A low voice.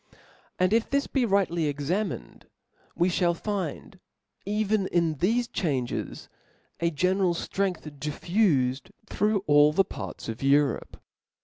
No: medium, 180 Hz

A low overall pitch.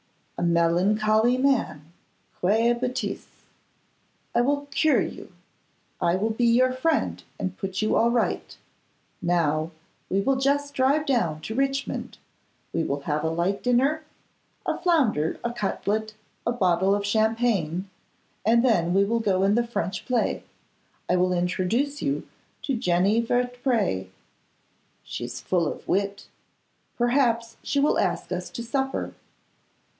No: high, 220 Hz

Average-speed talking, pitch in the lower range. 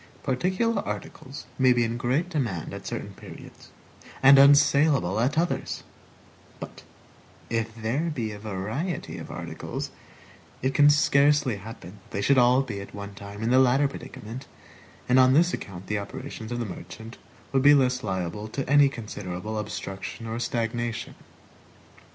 Yes: average, 155 wpm; low, 120 Hz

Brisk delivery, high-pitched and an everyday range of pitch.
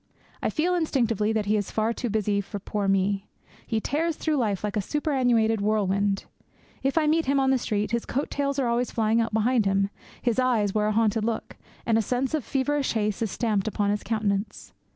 Yes: fast, 215 wpm; high, 225 Hz; average, 3.9 semitones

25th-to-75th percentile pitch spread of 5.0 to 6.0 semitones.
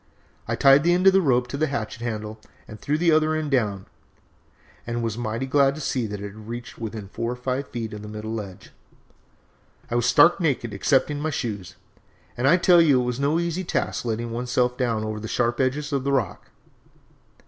No: average, 4.6 semitones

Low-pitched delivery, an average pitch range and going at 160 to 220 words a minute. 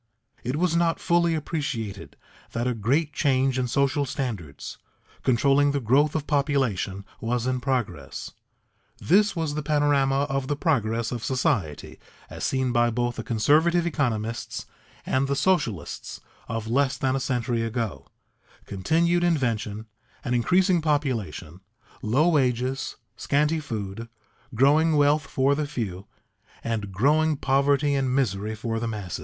No: low, 130 Hz; average, 4.5 semitones; average, 140 wpm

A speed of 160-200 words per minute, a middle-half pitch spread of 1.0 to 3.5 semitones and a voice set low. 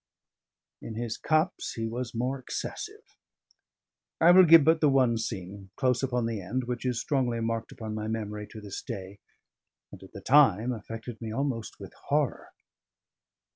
Yes: average, 165 wpm; average, 3.1 semitones; low, 115 Hz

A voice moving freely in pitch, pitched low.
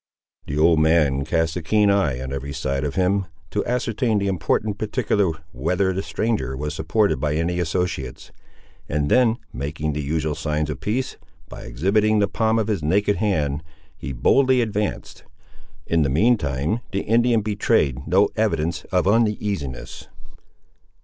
Yes: wide, 6.0 semitones; very low, 90 Hz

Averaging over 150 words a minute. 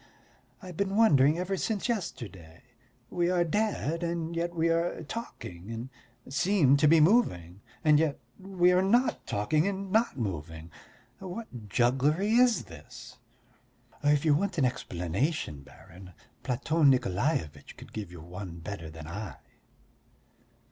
No: slow, 135 wpm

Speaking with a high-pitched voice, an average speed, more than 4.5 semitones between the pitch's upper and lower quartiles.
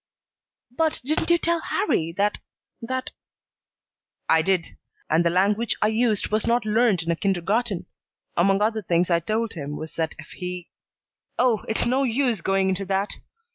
Yes: high, 205 Hz; average, 170 wpm; average, 5.0 semitones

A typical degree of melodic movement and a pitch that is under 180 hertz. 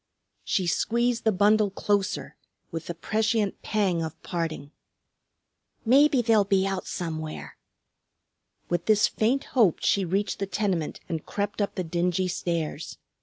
No: average, 3.9 semitones; high, 195 Hz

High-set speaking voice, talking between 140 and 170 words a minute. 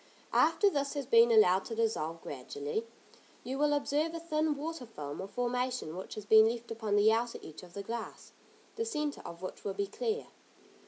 No: high, 230 Hz; average, 195 wpm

